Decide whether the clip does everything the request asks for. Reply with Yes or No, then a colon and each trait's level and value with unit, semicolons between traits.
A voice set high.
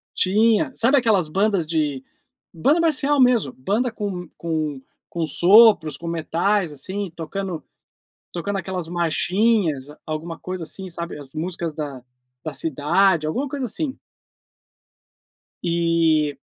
No: medium, 175 Hz